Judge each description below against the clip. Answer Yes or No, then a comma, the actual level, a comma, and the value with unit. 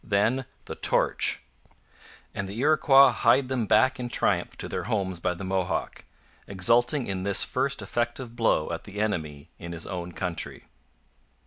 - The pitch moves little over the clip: No, average, 5.0 semitones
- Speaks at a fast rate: No, average, 155 wpm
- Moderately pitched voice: No, low, 105 Hz